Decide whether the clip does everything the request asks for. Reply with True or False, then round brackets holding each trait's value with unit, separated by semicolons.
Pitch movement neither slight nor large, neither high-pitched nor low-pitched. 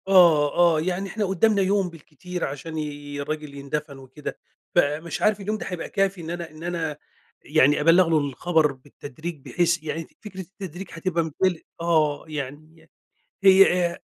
True (3.3 semitones; 165 Hz)